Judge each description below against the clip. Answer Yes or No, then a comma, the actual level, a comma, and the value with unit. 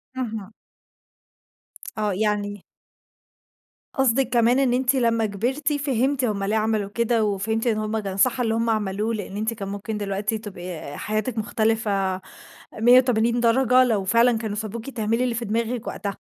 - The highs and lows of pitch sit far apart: No, narrow, 2.6 semitones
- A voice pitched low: No, high, 220 Hz